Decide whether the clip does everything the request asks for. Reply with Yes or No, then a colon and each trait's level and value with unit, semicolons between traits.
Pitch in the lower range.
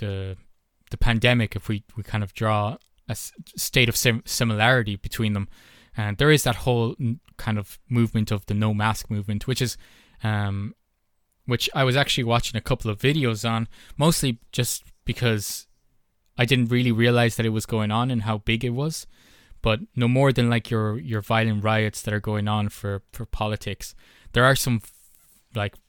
Yes: low, 110 Hz